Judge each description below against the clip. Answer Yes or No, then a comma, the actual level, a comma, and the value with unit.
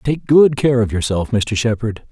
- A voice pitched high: No, low, 120 Hz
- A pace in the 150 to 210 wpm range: Yes, average, 200 wpm